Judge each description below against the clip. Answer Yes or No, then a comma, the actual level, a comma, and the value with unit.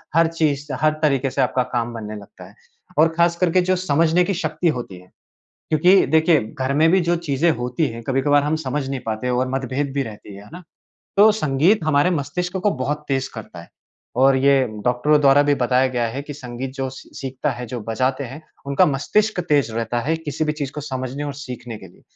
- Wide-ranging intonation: No, average, 3.7 semitones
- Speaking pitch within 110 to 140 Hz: Yes, low, 135 Hz